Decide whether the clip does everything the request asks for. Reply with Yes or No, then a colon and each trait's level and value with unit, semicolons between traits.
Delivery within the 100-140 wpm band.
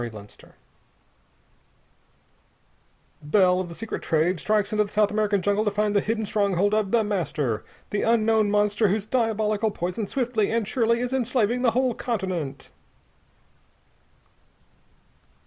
Yes: slow, 135 wpm